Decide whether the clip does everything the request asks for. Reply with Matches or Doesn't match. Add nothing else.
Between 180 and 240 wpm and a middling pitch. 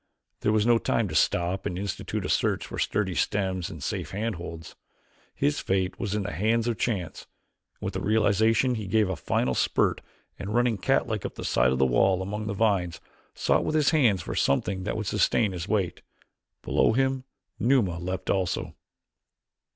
Doesn't match